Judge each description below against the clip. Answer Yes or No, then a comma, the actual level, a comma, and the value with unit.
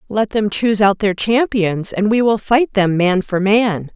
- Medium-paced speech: No, fast, 215 wpm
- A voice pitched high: Yes, high, 205 Hz